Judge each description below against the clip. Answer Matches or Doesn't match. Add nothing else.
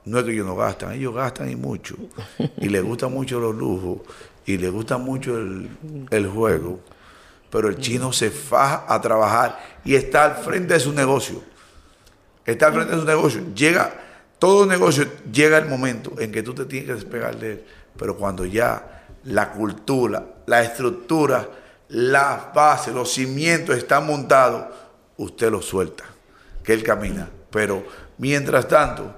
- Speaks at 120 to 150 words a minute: Doesn't match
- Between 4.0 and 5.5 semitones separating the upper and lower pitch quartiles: Matches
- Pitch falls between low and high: Doesn't match